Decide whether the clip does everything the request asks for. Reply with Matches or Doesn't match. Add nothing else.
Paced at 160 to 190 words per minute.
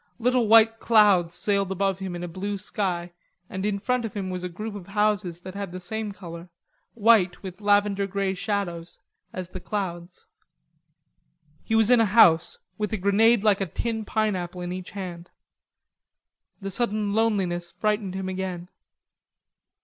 Matches